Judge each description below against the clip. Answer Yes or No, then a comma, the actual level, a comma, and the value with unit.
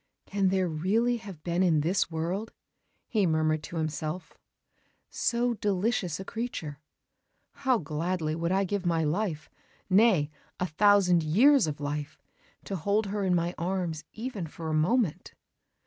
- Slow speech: No, average, 150 wpm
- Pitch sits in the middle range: Yes, medium, 180 Hz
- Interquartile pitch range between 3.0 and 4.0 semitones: No, average, 4.5 semitones